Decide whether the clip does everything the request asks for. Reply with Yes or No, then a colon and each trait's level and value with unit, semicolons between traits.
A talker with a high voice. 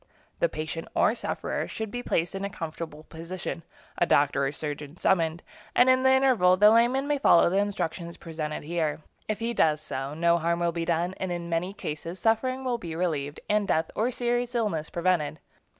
No: medium, 175 Hz